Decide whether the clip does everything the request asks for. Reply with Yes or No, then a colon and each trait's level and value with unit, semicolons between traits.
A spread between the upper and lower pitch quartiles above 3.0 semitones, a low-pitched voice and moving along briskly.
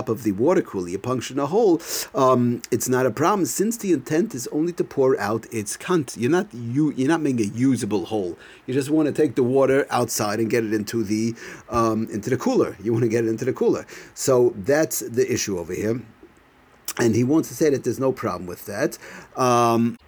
Yes: average, 3.8 semitones; low, 125 Hz; fast, 225 wpm